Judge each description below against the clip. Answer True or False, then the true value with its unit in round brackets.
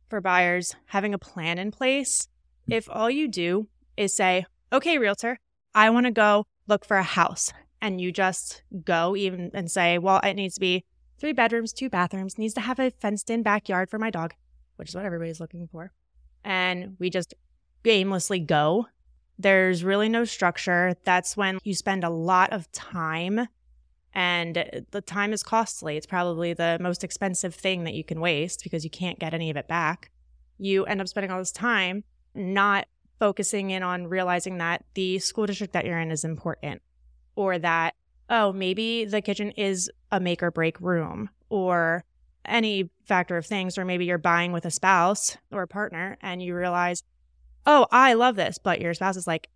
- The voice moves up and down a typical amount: True (3.3 semitones)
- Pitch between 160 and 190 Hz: True (185 Hz)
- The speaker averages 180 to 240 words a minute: True (190 wpm)